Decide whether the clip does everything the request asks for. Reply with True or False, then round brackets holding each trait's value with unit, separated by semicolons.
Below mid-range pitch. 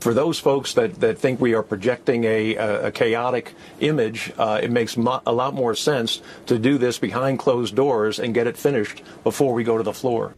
True (120 Hz)